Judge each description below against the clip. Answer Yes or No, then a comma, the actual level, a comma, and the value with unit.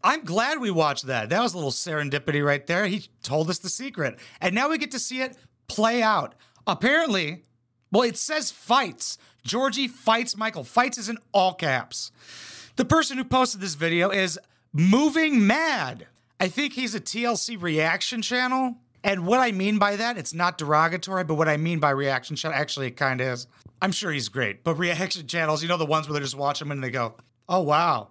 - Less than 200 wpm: No, fast, 205 wpm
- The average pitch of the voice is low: No, medium, 185 Hz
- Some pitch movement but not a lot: No, wide, 7.7 semitones